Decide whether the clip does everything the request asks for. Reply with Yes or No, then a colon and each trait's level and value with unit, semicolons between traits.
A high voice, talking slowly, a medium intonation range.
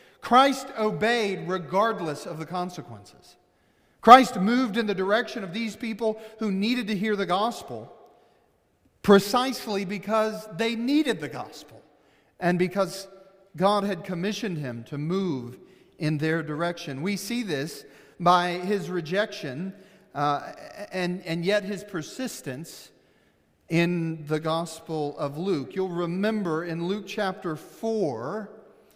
Yes: high, 195 Hz; slow, 125 wpm; average, 4.1 semitones